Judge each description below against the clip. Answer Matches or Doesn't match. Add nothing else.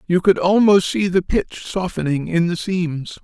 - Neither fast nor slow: Matches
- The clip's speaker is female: Doesn't match